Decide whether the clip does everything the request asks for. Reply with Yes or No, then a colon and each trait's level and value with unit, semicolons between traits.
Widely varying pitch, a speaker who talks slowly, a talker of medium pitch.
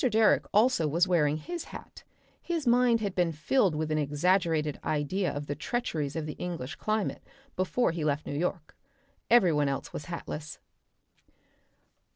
No: wide, 5.8 semitones; average, 160 wpm; medium, 165 Hz